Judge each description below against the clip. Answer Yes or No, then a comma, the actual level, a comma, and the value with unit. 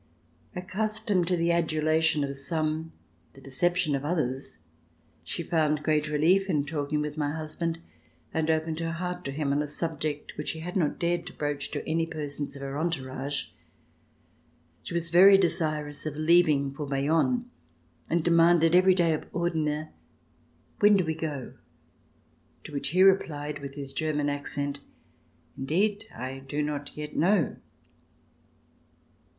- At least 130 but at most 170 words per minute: Yes, average, 150 wpm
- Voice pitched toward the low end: No, medium, 155 Hz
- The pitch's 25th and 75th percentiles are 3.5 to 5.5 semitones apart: No, average, 2.8 semitones